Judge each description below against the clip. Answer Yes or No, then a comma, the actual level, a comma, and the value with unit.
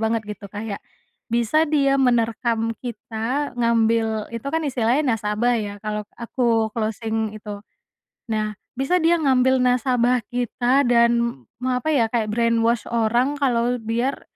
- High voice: Yes, high, 235 Hz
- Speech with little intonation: Yes, narrow, 2.3 semitones